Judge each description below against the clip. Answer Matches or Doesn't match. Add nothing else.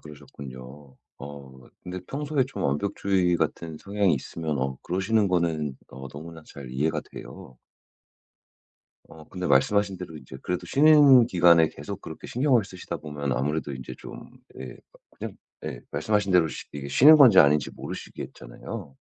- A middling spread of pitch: Doesn't match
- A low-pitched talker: Matches